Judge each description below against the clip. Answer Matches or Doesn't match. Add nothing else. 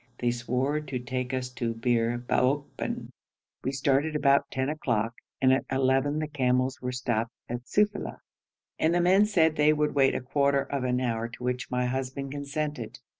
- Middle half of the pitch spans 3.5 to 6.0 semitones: Doesn't match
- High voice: Doesn't match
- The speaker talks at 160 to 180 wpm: Matches